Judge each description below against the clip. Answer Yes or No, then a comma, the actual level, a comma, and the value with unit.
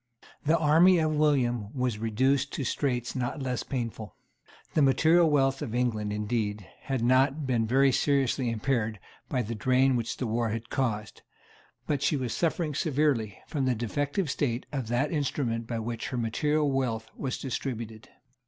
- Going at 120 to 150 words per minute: No, average, 160 wpm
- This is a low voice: Yes, low, 130 Hz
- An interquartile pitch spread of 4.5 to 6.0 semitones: No, average, 3.7 semitones